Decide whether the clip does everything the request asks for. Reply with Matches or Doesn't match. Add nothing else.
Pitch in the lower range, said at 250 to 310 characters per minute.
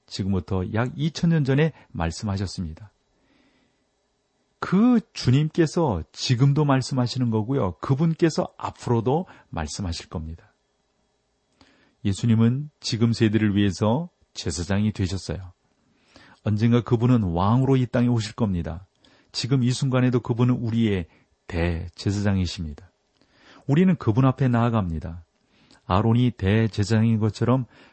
Matches